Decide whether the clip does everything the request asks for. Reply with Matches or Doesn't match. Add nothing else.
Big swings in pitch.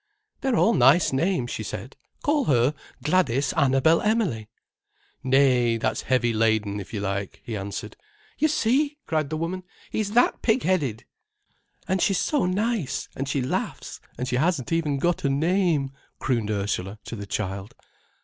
Matches